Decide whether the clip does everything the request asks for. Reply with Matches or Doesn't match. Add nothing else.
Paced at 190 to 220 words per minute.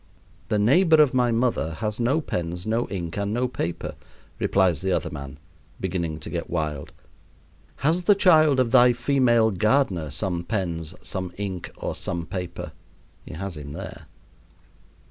Doesn't match